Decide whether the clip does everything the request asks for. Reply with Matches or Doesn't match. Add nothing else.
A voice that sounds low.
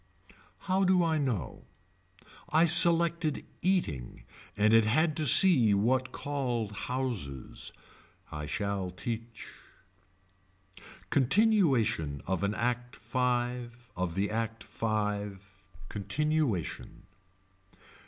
Matches